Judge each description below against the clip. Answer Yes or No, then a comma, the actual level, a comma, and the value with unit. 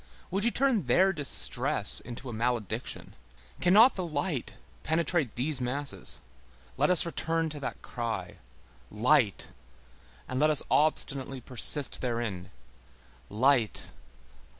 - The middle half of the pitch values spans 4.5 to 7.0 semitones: Yes, average, 5.1 semitones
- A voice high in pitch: No, medium, 140 Hz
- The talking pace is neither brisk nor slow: No, slow, 115 wpm